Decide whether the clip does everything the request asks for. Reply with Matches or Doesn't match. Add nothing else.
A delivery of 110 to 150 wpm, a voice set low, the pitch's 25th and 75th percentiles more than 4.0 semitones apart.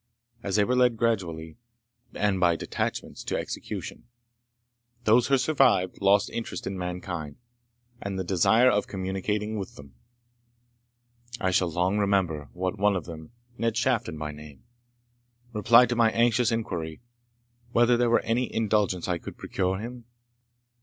Matches